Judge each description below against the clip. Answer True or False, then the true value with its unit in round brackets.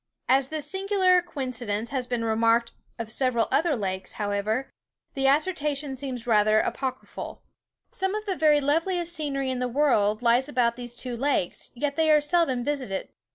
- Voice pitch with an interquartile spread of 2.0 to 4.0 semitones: False (4.4 semitones)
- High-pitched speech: True (265 Hz)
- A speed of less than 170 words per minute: True (160 wpm)